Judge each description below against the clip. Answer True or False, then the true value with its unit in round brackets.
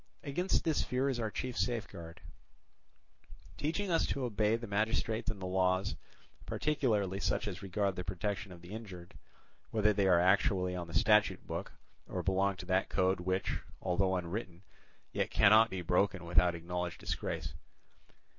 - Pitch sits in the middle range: False (95 Hz)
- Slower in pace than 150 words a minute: False (155 wpm)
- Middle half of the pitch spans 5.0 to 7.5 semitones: False (3.5 semitones)